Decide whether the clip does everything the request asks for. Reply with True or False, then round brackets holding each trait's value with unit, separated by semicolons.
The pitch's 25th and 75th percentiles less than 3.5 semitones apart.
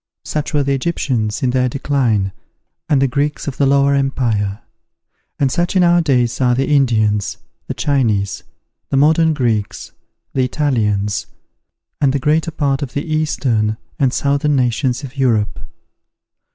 False (3.8 semitones)